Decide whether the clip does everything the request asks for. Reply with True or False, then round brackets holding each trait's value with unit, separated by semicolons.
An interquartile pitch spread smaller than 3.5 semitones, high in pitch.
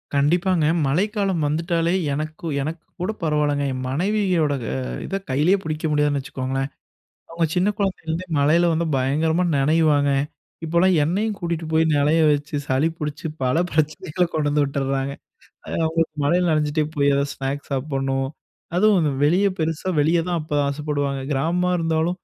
False (3.1 semitones; 155 Hz)